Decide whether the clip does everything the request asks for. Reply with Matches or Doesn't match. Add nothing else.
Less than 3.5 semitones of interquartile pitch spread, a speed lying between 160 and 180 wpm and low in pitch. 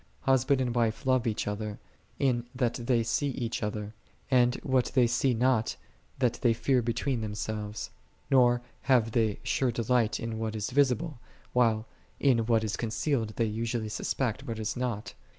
Matches